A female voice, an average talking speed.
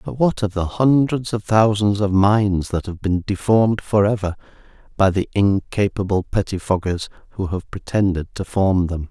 No: male; average, 165 wpm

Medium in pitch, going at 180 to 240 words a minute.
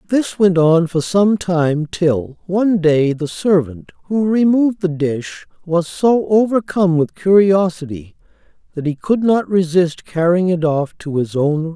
No: medium, 175 Hz; average, 165 wpm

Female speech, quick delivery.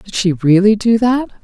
Yes: female; fast, 210 wpm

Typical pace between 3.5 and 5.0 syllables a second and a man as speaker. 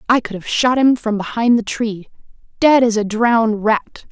No: 4.8 syllables/s; female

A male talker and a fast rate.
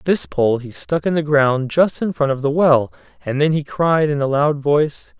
Yes: male; fast, 245 wpm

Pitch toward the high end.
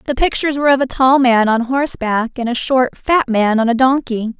Yes: very high, 250 Hz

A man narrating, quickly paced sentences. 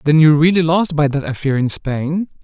Yes: male; fast, 220 wpm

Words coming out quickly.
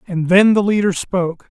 No: average, 190 wpm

